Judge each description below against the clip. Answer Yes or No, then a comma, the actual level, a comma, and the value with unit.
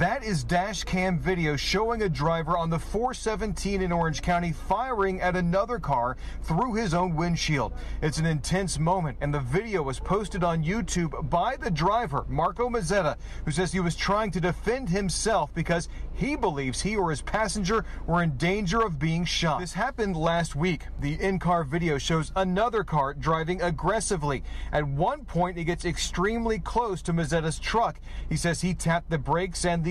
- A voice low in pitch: No, medium, 175 Hz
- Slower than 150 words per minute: No, average, 180 wpm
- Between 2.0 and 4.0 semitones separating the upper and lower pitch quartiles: Yes, average, 3.1 semitones